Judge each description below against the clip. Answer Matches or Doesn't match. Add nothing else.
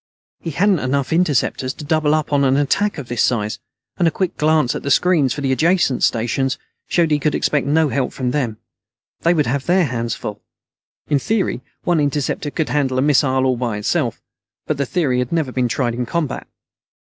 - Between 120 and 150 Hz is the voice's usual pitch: Matches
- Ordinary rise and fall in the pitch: Matches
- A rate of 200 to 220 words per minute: Matches